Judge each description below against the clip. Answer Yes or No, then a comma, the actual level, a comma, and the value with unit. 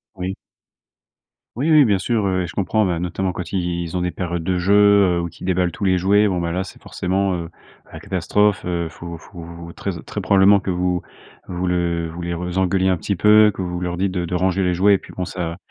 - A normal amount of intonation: No, narrow, 2.0 semitones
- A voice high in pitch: No, very low, 90 Hz